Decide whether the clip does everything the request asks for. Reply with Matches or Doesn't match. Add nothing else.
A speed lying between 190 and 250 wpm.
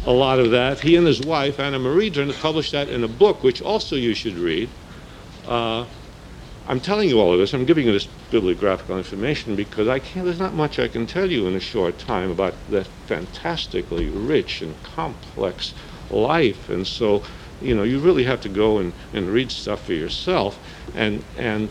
Matches